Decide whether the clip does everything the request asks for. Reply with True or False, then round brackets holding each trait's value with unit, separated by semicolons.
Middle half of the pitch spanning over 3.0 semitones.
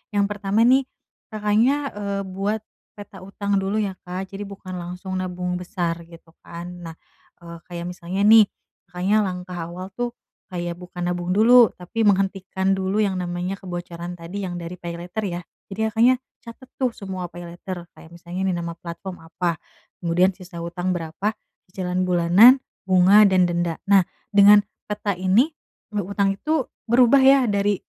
False (2.7 semitones)